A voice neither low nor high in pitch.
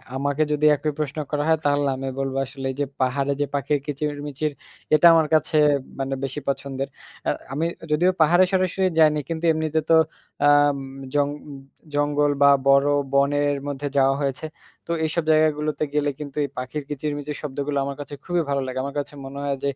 Yes: medium, 145 Hz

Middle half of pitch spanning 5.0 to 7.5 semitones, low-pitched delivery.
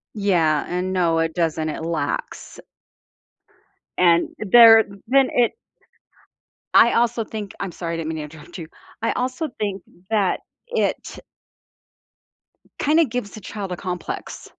No: average, 5.3 semitones; high, 190 Hz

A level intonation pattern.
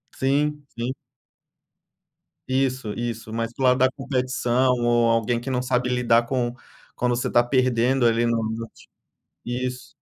Yes: narrow, 1.6 semitones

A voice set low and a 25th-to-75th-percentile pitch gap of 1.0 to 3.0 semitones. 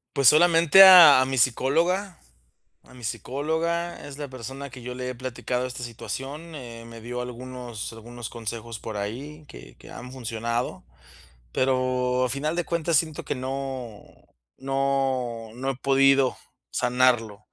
Yes: low, 130 Hz; average, 2.7 semitones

